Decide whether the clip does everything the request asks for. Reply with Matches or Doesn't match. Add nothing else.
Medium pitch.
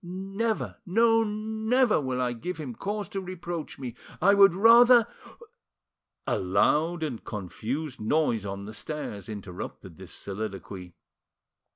Matches